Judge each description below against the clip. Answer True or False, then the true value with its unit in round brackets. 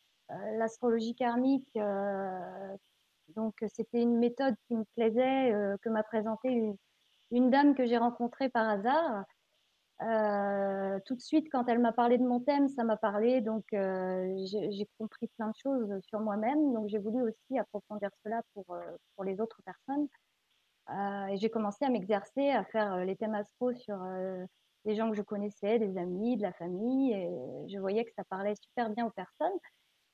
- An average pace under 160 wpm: False (180 wpm)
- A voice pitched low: False (220 Hz)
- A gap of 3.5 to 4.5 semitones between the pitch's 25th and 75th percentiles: False (3.1 semitones)